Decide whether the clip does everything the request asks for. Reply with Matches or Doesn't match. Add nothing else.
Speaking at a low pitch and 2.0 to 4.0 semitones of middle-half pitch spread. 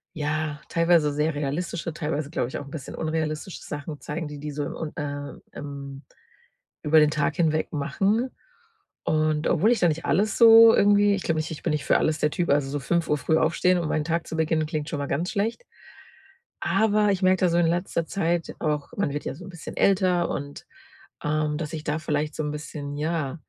Doesn't match